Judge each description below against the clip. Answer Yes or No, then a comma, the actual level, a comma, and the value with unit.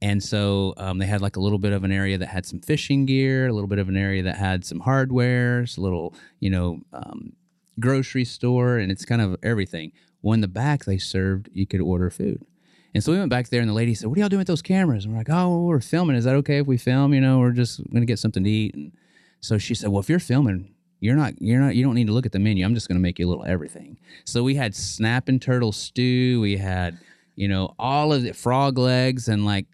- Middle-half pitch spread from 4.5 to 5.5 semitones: Yes, average, 5.2 semitones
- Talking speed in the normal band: No, fast, 270 wpm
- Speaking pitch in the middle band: No, low, 115 Hz